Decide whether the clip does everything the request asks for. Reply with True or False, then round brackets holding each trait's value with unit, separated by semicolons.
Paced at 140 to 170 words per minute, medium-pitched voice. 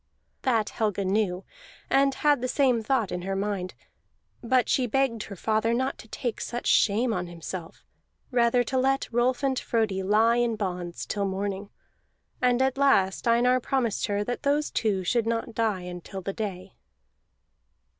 False (165 wpm; 225 Hz)